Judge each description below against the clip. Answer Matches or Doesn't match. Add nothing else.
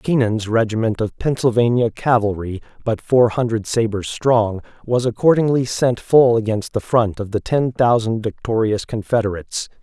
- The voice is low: Matches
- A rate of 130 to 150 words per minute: Matches